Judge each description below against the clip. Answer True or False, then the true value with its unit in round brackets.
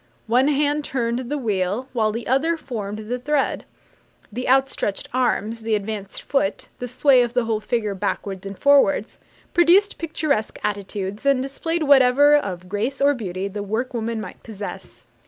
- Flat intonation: False (4.8 semitones)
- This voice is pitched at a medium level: False (240 Hz)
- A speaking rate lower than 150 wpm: False (160 wpm)